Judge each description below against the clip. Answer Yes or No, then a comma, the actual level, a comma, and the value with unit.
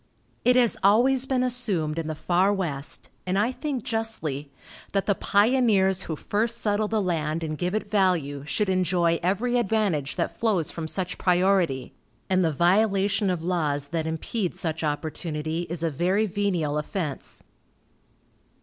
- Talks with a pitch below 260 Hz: Yes, medium, 185 Hz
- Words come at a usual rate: Yes, average, 155 wpm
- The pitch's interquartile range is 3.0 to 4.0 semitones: No, average, 4.7 semitones